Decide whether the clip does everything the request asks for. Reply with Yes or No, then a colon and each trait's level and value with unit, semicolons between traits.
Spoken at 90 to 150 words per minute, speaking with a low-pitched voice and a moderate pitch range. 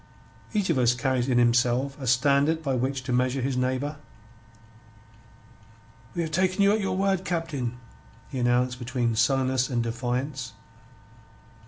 Yes: average, 145 wpm; low, 130 Hz; average, 3.4 semitones